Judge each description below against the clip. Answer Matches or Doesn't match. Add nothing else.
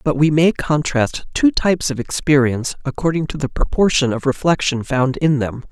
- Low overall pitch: Doesn't match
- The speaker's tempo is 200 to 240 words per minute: Doesn't match